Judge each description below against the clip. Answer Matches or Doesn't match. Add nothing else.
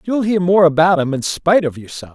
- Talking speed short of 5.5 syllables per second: Doesn't match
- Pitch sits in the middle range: Matches